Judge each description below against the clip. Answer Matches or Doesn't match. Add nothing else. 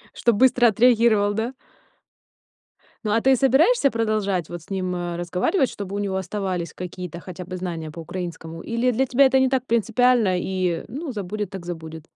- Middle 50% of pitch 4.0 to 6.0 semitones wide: Matches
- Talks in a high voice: Matches